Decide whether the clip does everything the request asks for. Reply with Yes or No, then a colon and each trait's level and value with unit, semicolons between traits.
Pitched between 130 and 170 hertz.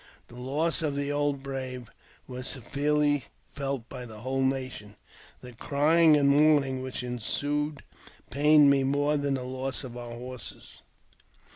Yes: low, 135 Hz